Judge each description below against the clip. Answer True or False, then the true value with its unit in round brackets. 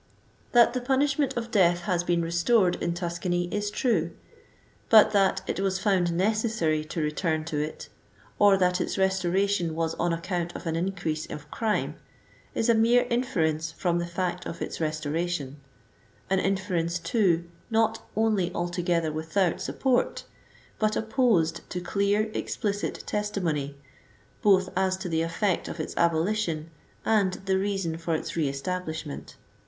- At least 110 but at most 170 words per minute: True (150 wpm)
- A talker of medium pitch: True (180 Hz)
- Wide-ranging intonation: False (3.7 semitones)